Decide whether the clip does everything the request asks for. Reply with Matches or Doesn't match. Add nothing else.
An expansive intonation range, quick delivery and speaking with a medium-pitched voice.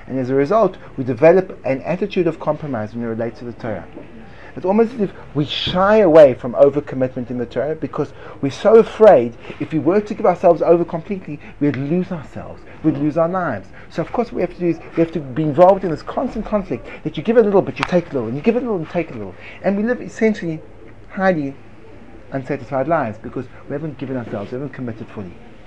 Matches